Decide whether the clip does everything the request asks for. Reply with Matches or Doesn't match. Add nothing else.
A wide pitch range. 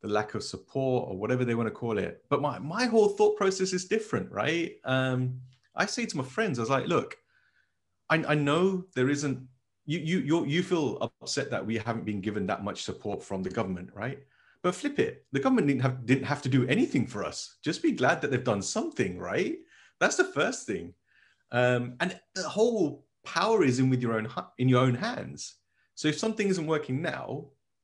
Matches